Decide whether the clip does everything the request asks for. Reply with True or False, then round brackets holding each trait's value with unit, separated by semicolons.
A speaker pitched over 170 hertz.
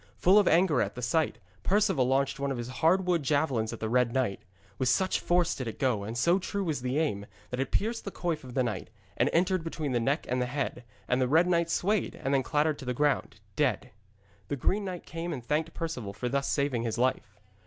False (140 Hz)